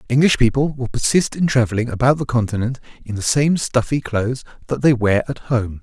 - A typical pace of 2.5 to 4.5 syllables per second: No, 5.7 syllables/s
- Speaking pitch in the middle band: No, low, 125 Hz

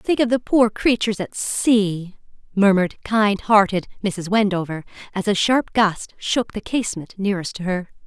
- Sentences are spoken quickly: No, average, 165 wpm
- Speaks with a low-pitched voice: No, high, 200 Hz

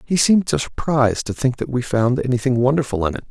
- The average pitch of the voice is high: No, low, 130 Hz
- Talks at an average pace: No, fast, 220 wpm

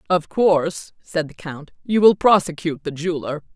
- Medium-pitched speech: Yes, medium, 170 Hz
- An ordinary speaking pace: Yes, average, 170 wpm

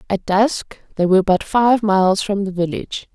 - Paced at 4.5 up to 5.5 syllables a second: Yes, 5.0 syllables/s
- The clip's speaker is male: No, female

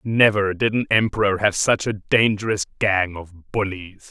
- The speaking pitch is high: No, low, 100 Hz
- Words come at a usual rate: Yes, average, 160 wpm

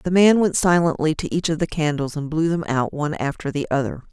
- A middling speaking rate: No, fast, 250 wpm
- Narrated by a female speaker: Yes, female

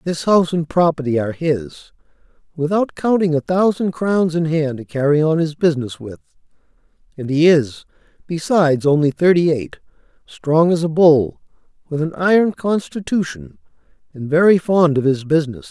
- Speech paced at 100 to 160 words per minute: Yes, average, 155 wpm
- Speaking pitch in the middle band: Yes, medium, 160 Hz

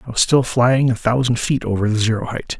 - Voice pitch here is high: No, low, 120 Hz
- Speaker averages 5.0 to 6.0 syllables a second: Yes, 5.7 syllables/s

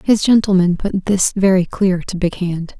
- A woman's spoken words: Yes, female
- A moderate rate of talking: Yes, average, 195 wpm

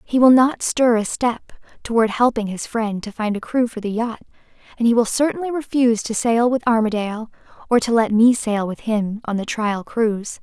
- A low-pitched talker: No, high, 230 Hz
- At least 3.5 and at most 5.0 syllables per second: No, 5.3 syllables/s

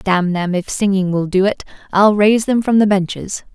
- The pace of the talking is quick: Yes, fast, 220 wpm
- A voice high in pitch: Yes, high, 195 Hz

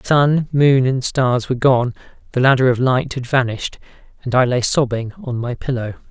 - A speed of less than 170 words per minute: No, average, 185 wpm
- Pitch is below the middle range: Yes, low, 125 Hz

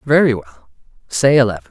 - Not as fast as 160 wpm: Yes, average, 140 wpm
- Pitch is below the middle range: Yes, low, 120 Hz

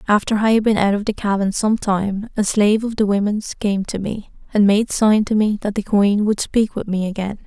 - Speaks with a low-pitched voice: No, high, 205 Hz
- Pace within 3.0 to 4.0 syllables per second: No, 5.2 syllables/s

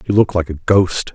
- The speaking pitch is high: No, very low, 90 Hz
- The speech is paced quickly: Yes, fast, 260 wpm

